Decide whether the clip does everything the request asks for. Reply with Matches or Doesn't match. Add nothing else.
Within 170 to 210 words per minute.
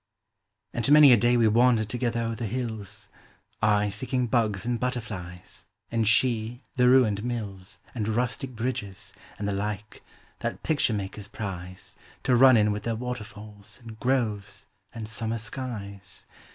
Doesn't match